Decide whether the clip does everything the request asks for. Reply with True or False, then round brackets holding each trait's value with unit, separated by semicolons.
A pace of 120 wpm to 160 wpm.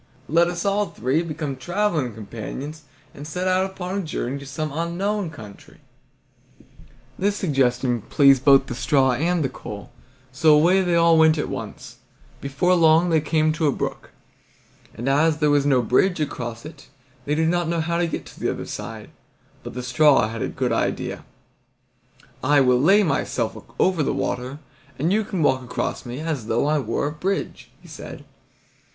False (180 wpm)